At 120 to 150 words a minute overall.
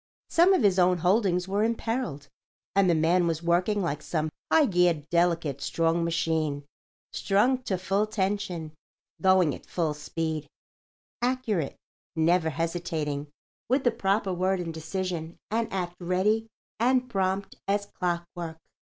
Yes: slow, 135 wpm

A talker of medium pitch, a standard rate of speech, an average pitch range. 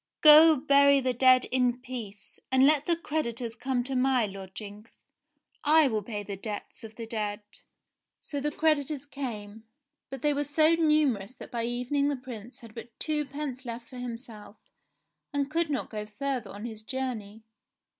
No: very high, 255 Hz; average, 165 wpm; average, 4.3 semitones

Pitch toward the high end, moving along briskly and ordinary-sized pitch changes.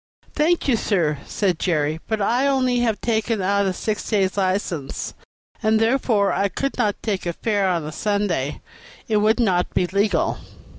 No: high, 200 Hz; average, 170 wpm; average, 3.6 semitones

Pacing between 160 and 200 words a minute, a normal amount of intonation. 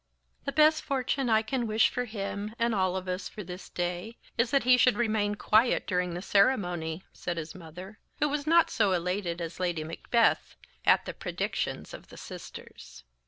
Yes: average, 185 wpm; average, 5.0 semitones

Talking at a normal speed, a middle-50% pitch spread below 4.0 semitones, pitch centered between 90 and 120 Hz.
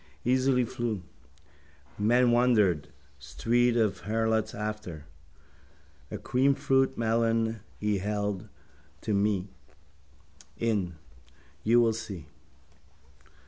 No: slow, 85 wpm; average, 2.8 semitones; low, 110 Hz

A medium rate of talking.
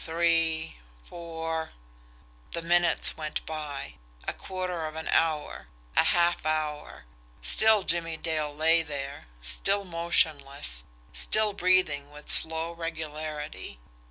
No: slow, 110 wpm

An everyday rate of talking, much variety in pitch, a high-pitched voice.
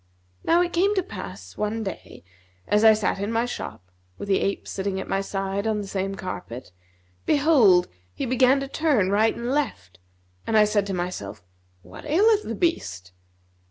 Yes: average, 180 wpm; wide, 6.0 semitones; high, 205 Hz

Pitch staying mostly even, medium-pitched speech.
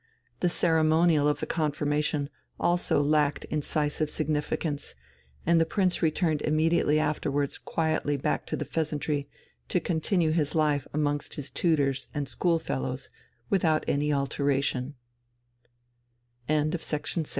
Yes: narrow, 1.8 semitones; medium, 150 Hz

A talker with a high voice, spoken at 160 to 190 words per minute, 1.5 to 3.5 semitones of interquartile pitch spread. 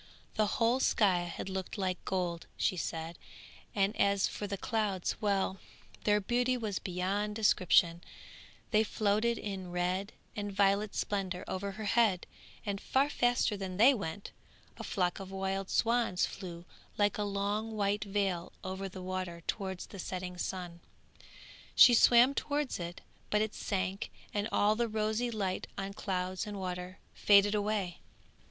No: high, 200 Hz; average, 150 wpm; narrow, 2.4 semitones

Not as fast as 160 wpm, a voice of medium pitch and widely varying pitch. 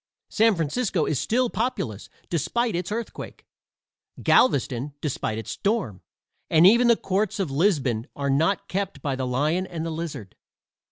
Yes: average, 150 wpm; medium, 165 Hz; wide, 6.8 semitones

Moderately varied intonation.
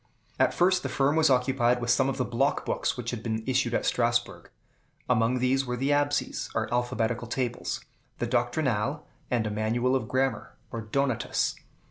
No: narrow, 2.3 semitones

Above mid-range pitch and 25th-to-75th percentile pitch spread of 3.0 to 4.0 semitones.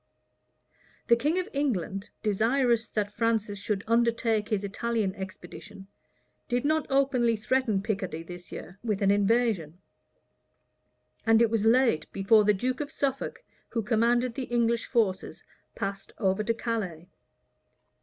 Yes: high, 225 Hz; average, 3.3 semitones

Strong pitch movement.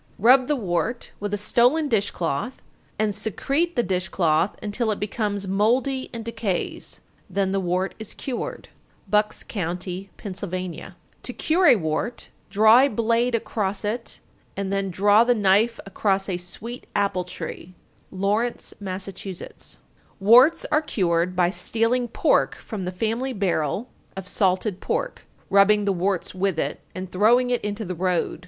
No: average, 3.9 semitones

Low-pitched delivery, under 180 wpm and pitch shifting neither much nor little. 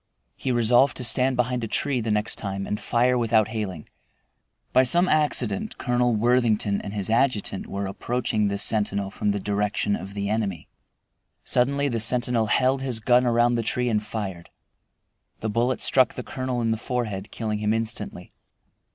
Yes: low, 115 Hz; average, 170 wpm; average, 3.1 semitones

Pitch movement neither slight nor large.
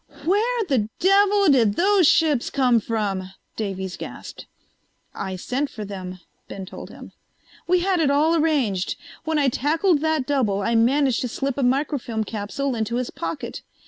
No: wide, 6.6 semitones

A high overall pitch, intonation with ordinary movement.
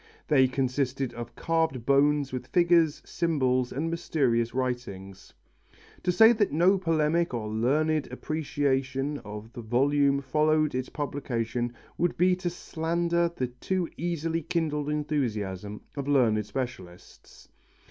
No: medium, 140 Hz; average, 4.7 semitones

